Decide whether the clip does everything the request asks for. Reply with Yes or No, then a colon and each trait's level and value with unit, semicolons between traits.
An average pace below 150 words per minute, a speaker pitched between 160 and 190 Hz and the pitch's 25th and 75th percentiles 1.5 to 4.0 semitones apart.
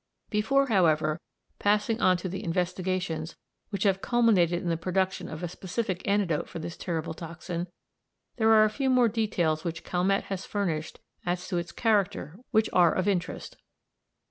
No: average, 165 wpm; medium, 185 Hz; average, 3.4 semitones